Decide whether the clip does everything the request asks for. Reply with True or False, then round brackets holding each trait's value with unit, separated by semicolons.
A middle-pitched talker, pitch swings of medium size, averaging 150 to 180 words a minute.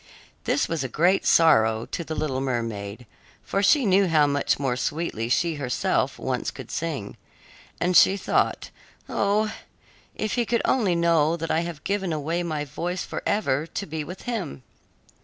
True (165 Hz; 4.9 semitones; 165 wpm)